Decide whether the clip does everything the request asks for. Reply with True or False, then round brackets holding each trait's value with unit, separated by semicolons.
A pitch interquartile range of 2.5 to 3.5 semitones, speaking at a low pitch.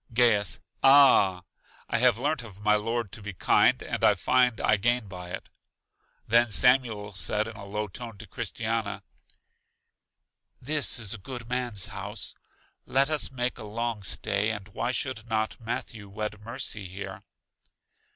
True (3.0 semitones; 110 Hz)